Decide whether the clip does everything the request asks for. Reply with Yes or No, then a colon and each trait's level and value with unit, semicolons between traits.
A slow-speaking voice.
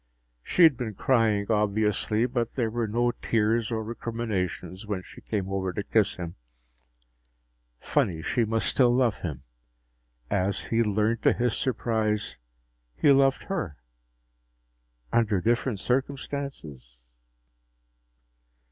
Yes: slow, 120 wpm